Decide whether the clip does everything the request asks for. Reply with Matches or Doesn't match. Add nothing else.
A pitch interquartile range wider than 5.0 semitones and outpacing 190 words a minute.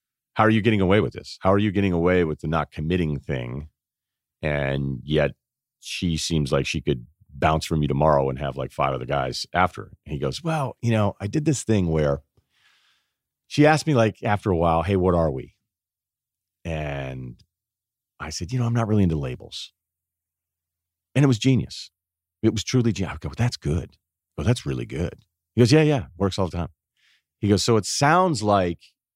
Matches